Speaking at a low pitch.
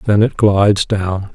Yes: low, 100 Hz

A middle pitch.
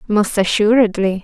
No: high, 210 Hz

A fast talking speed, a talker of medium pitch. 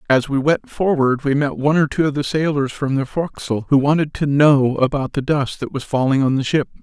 Yes: fast, 245 wpm; medium, 145 Hz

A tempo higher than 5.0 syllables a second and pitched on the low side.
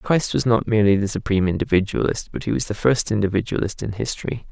Yes: 6.5 syllables/s; low, 105 Hz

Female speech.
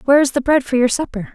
Yes: female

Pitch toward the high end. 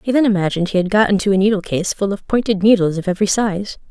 Yes: high, 200 Hz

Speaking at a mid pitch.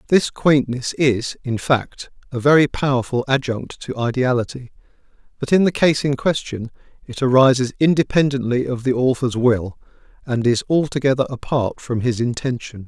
No: low, 130 Hz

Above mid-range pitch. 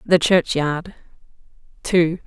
No: medium, 170 Hz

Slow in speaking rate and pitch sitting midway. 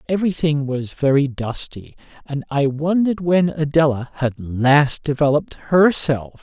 Yes: slow, 120 wpm; medium, 145 Hz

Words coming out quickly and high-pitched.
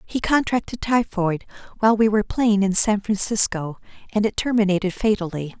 No: average, 150 wpm; high, 205 Hz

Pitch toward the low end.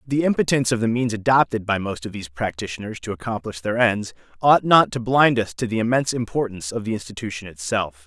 Yes: low, 110 Hz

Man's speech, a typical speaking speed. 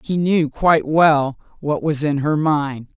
No: female; average, 180 wpm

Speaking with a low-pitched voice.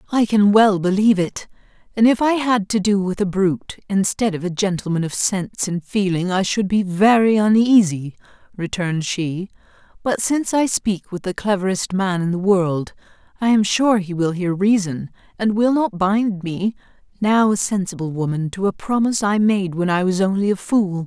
No: high, 195 Hz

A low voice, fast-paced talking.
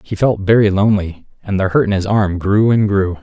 Yes: low, 100 Hz; fast, 240 wpm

